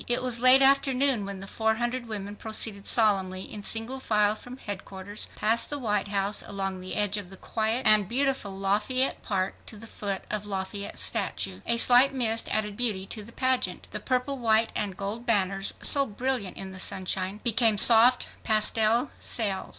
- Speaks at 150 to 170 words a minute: No, average, 180 wpm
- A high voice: Yes, high, 215 Hz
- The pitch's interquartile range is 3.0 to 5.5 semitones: Yes, average, 3.5 semitones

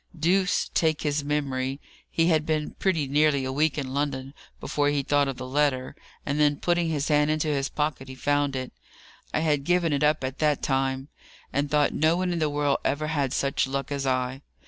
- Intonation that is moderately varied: No, narrow, 2.1 semitones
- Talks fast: Yes, fast, 210 wpm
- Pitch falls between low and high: Yes, medium, 145 Hz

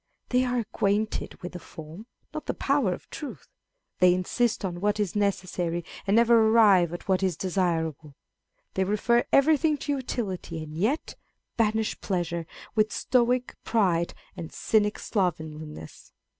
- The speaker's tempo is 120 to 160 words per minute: Yes, average, 145 wpm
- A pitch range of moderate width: Yes, average, 5.0 semitones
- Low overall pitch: No, high, 200 Hz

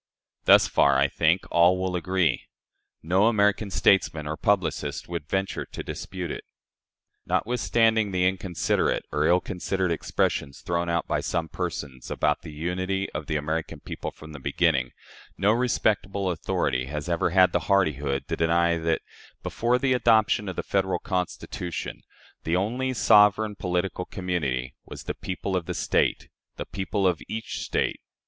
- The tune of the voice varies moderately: Yes, average, 3.4 semitones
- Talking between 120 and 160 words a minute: Yes, average, 155 wpm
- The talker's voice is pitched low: Yes, very low, 90 Hz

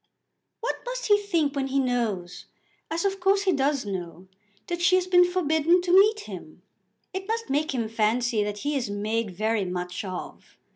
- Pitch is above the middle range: Yes, very high, 280 Hz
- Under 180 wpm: No, average, 185 wpm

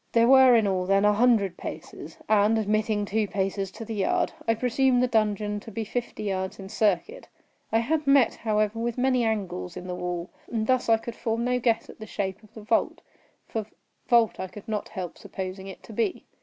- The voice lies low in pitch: No, high, 215 Hz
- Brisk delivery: Yes, fast, 210 wpm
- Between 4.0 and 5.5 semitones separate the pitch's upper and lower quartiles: No, average, 2.9 semitones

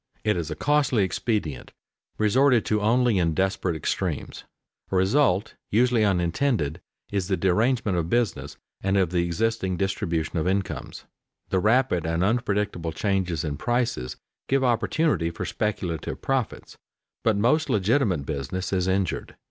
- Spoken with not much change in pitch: No, average, 5.1 semitones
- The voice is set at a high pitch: No, low, 100 Hz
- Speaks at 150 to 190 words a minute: No, average, 140 wpm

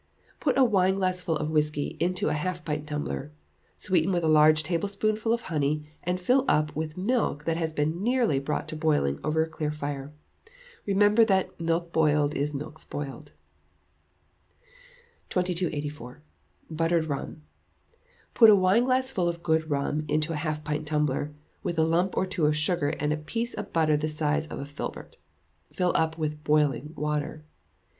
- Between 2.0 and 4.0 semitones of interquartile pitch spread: Yes, average, 3.3 semitones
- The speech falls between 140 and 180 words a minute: Yes, average, 165 wpm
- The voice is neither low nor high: Yes, medium, 155 Hz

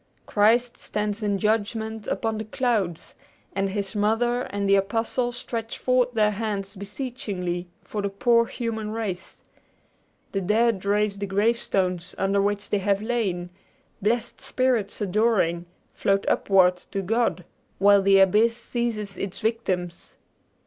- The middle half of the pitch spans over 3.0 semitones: No, narrow, 2.6 semitones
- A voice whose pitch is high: Yes, high, 210 Hz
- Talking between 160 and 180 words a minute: No, slow, 135 wpm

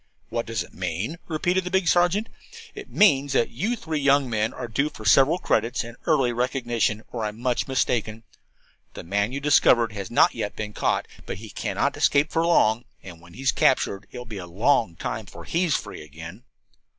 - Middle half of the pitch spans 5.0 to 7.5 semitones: Yes, wide, 5.4 semitones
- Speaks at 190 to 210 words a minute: Yes, fast, 205 wpm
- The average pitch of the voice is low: Yes, low, 120 Hz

